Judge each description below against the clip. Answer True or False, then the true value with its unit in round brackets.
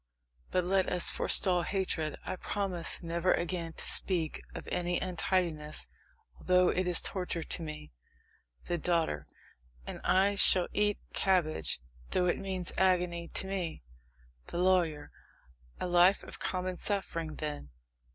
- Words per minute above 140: False (135 wpm)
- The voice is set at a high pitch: False (180 Hz)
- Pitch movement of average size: False (1.9 semitones)